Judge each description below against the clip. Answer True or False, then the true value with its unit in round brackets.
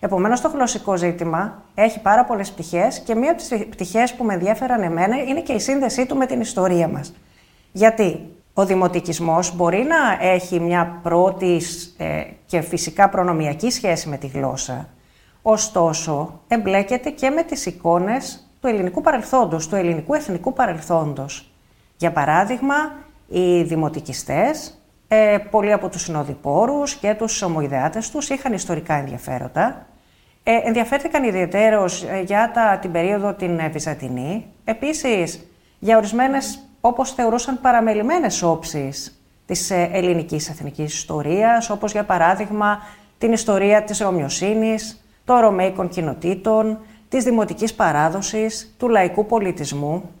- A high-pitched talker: True (195 Hz)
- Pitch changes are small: False (5.3 semitones)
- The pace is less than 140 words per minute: True (130 wpm)